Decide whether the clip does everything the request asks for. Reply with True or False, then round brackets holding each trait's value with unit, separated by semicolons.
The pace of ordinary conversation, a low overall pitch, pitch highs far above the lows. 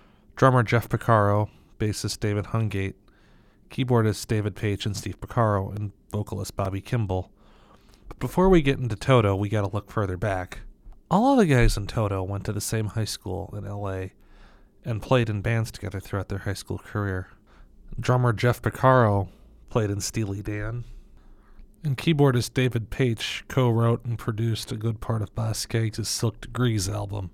False (160 wpm; 110 Hz; 2.8 semitones)